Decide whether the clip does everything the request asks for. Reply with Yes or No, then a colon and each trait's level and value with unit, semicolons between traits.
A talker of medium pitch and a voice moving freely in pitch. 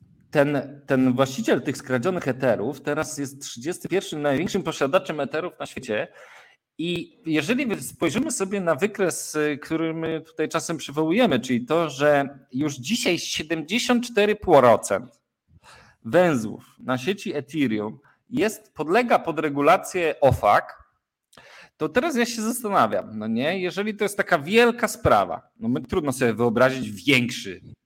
Yes: medium, 160 Hz; wide, 5.9 semitones